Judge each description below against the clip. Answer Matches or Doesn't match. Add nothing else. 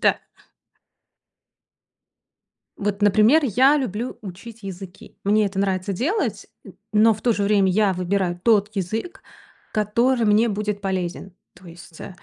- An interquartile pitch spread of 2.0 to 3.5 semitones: Matches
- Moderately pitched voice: Doesn't match